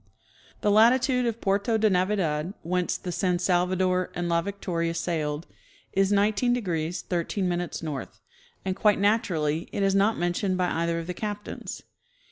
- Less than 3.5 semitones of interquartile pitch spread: Yes, average, 3.1 semitones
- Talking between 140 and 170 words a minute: Yes, average, 145 wpm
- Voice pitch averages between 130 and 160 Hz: No, medium, 185 Hz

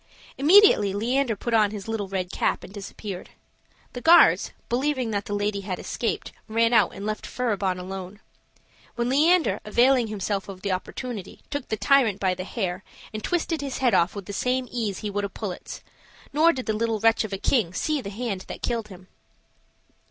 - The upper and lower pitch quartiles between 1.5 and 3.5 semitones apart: No, average, 4.2 semitones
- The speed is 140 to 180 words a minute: No, average, 190 wpm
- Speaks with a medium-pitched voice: No, high, 215 Hz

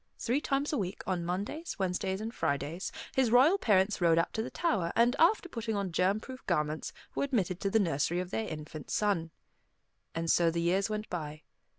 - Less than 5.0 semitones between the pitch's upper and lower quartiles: No, average, 5.3 semitones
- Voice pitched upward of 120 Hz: Yes, high, 190 Hz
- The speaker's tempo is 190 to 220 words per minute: Yes, average, 200 wpm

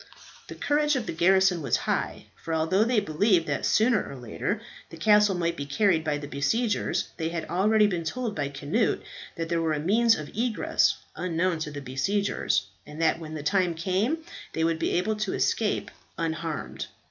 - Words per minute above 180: Yes, average, 190 wpm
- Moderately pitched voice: Yes, medium, 170 Hz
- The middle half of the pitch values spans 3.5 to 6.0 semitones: Yes, average, 4.9 semitones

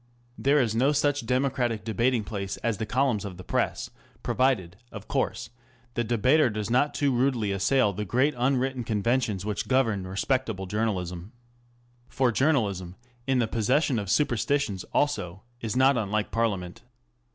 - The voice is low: Yes, low, 115 Hz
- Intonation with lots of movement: No, average, 4.4 semitones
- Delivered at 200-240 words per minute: No, average, 155 wpm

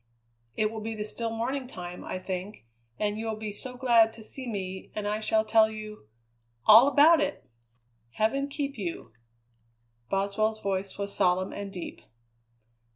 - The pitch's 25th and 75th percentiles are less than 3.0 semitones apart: Yes, narrow, 2.6 semitones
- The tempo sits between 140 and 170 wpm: Yes, average, 160 wpm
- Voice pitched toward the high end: Yes, high, 215 Hz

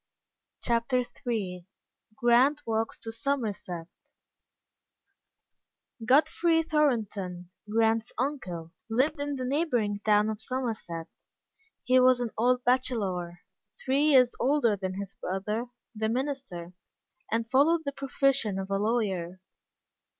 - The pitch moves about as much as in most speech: Yes, average, 4.9 semitones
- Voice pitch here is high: Yes, high, 230 Hz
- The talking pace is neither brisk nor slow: No, slow, 110 wpm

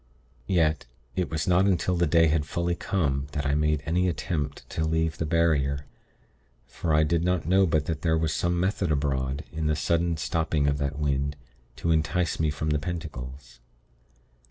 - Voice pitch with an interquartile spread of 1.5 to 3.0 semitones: Yes, average, 2.7 semitones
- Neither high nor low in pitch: No, very low, 80 Hz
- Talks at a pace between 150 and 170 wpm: No, average, 180 wpm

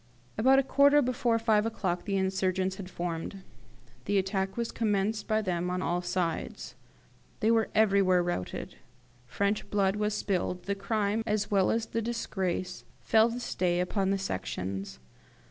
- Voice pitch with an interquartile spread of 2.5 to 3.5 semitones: Yes, average, 3.2 semitones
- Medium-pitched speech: No, high, 195 Hz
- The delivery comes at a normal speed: Yes, average, 155 wpm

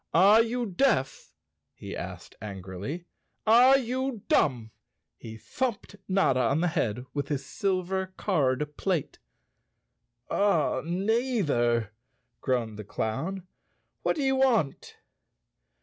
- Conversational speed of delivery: No, slow, 110 wpm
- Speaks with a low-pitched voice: No, medium, 175 Hz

